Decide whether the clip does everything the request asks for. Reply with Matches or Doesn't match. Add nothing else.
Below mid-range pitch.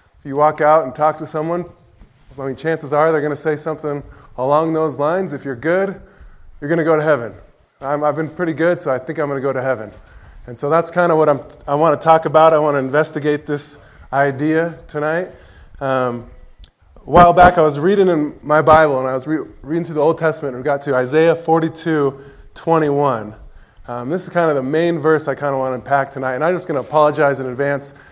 Doesn't match